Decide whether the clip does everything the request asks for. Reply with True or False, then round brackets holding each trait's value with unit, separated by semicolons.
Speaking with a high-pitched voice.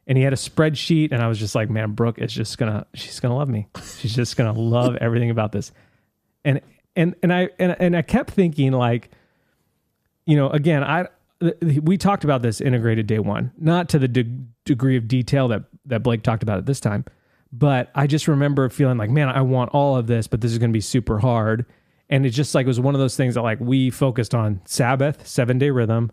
False (130 Hz)